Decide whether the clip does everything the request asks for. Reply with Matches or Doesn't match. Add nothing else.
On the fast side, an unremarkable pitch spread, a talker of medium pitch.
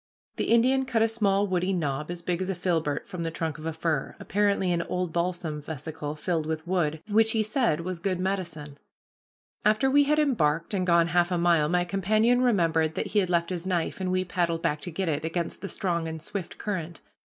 Matches